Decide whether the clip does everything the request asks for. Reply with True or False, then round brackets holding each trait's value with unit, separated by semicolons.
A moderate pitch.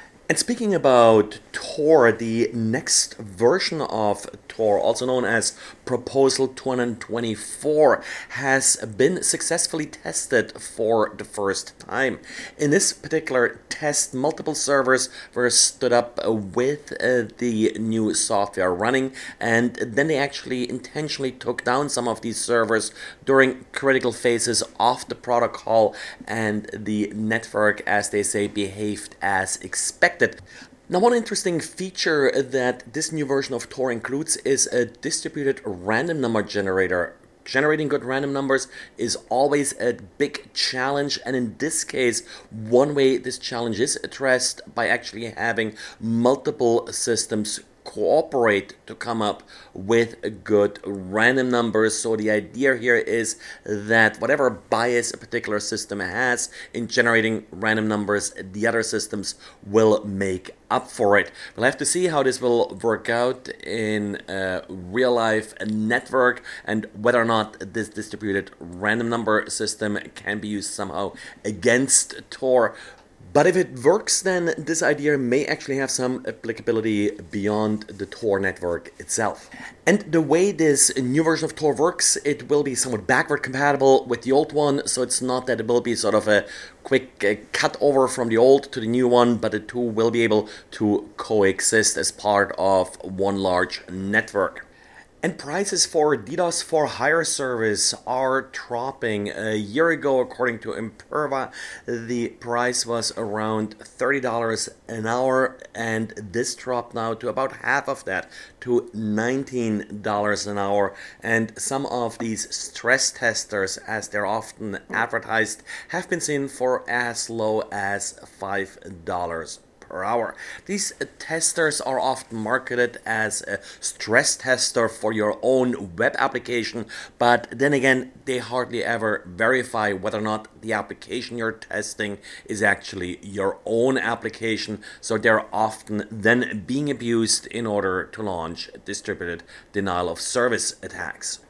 False (120 Hz)